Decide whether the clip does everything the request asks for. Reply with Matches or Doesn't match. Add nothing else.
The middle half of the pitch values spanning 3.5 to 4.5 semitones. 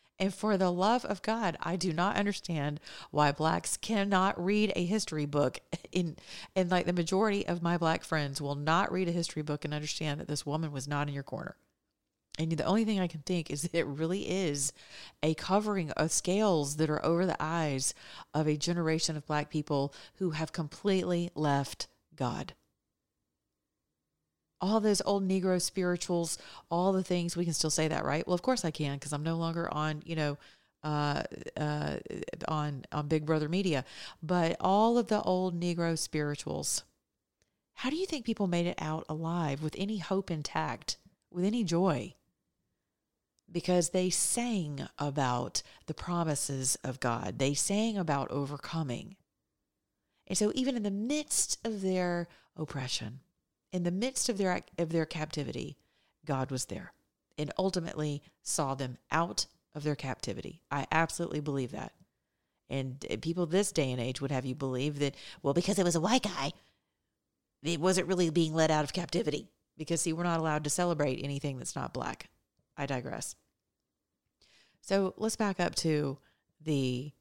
Matches